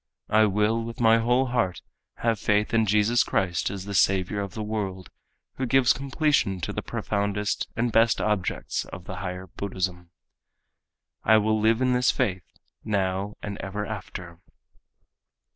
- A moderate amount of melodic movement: Yes, average, 3.2 semitones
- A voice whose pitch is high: No, low, 105 Hz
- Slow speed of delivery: No, average, 155 wpm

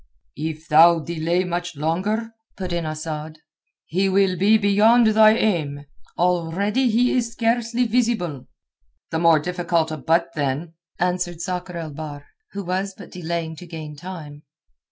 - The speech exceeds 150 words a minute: No, average, 145 wpm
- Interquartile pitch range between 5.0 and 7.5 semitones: No, average, 4.0 semitones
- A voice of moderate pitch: Yes, medium, 175 Hz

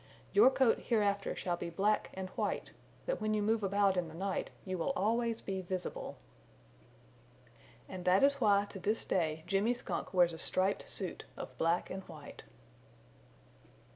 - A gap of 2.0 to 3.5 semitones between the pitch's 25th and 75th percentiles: Yes, average, 3.0 semitones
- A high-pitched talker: Yes, high, 195 Hz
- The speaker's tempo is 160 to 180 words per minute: Yes, average, 170 wpm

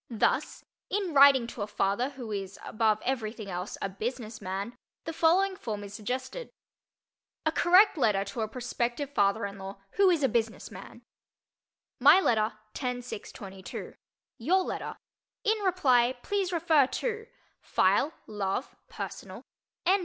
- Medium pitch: No, high, 245 Hz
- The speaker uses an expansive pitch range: Yes, wide, 7.6 semitones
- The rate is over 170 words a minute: No, average, 145 wpm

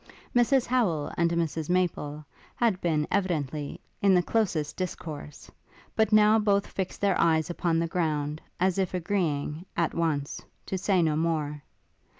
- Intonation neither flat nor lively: Yes, average, 4.0 semitones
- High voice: No, medium, 170 Hz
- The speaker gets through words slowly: No, average, 150 wpm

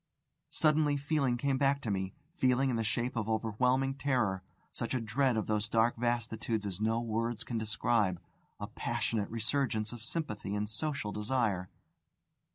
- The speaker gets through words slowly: No, average, 160 wpm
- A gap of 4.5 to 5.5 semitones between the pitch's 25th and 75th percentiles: No, average, 3.6 semitones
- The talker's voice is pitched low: Yes, low, 115 Hz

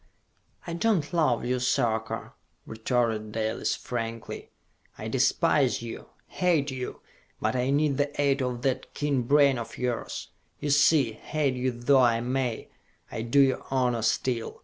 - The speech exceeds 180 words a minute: No, average, 150 wpm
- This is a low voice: Yes, low, 130 Hz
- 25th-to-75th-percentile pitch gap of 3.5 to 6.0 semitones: No, average, 3.1 semitones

